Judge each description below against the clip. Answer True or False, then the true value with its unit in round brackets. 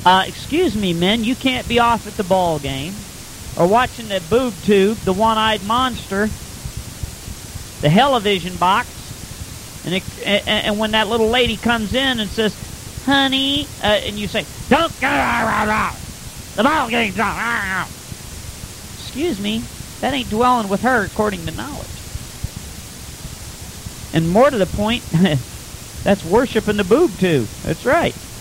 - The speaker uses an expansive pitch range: False (4.7 semitones)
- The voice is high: True (210 Hz)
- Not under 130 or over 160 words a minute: True (150 wpm)